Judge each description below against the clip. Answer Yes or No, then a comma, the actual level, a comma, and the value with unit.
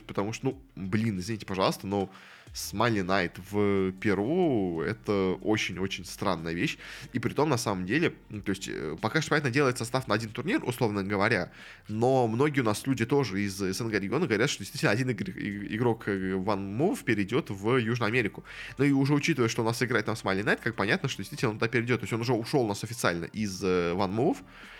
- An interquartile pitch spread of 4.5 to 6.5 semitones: No, average, 4.0 semitones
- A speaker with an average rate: No, fast, 200 wpm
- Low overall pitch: Yes, low, 110 Hz